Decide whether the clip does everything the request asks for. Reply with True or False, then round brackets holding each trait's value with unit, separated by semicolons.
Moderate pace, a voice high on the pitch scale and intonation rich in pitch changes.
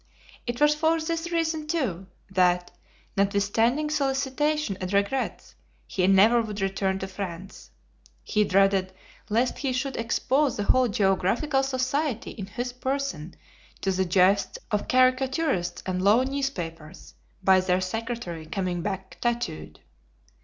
False (130 wpm; 210 Hz; 6.0 semitones)